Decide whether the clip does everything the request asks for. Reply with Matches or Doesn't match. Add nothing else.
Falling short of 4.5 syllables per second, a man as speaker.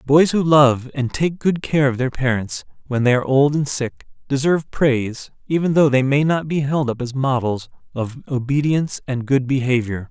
Doesn't match